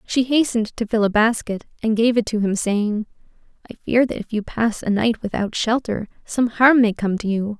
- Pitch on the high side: Yes, high, 220 Hz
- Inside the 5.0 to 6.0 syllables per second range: Yes, 5.2 syllables/s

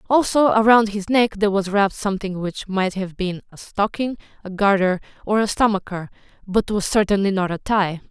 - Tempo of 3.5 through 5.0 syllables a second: No, 5.5 syllables/s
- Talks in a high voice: Yes, high, 200 Hz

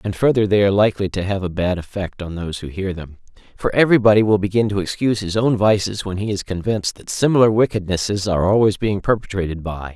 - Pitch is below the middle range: Yes, low, 100 Hz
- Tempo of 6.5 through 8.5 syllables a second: Yes, 6.6 syllables/s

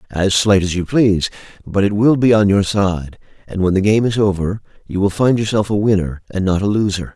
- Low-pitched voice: Yes, low, 100 Hz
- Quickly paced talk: Yes, fast, 235 wpm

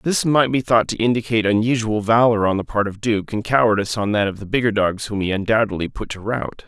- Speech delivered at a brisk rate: Yes, fast, 245 wpm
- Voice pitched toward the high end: No, low, 110 Hz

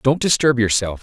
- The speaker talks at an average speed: Yes, average, 175 wpm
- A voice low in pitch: Yes, low, 125 Hz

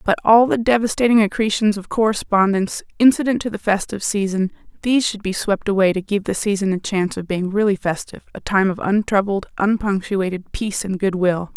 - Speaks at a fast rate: No, average, 185 wpm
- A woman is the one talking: Yes, female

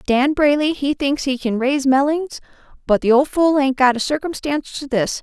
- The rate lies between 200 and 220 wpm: Yes, fast, 205 wpm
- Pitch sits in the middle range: No, very high, 275 Hz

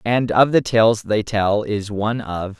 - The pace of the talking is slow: No, fast, 210 wpm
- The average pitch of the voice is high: No, low, 110 Hz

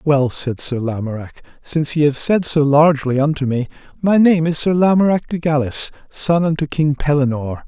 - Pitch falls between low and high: Yes, medium, 150 Hz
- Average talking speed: Yes, average, 180 wpm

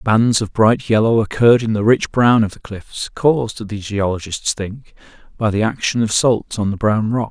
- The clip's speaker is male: Yes, male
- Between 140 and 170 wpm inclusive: No, fast, 205 wpm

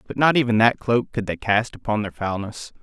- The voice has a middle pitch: No, low, 115 Hz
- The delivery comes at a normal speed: No, fast, 235 wpm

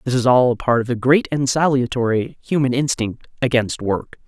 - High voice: No, low, 125 Hz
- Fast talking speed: No, average, 195 wpm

